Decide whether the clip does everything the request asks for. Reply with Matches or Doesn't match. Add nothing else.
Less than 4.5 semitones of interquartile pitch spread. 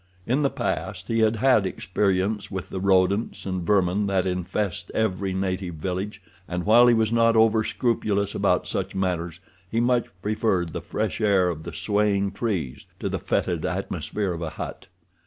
Matches